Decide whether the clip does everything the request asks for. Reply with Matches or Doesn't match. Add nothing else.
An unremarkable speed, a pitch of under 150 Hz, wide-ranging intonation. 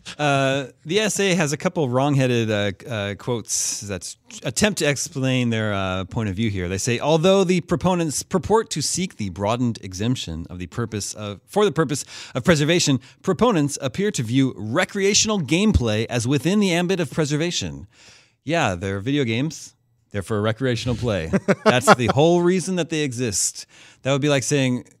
Matches